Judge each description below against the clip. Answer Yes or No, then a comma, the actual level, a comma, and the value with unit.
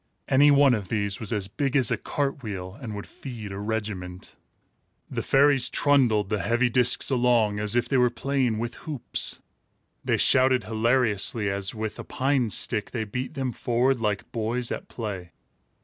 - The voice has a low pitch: Yes, low, 115 Hz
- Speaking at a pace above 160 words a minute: Yes, average, 175 wpm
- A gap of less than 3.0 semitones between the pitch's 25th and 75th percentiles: No, average, 3.7 semitones